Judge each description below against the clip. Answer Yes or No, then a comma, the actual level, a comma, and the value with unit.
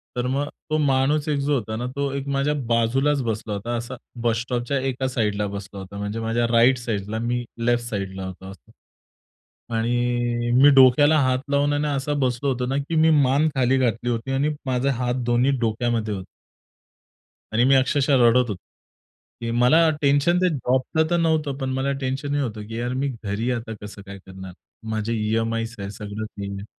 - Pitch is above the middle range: No, low, 120 Hz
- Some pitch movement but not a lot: Yes, average, 3.5 semitones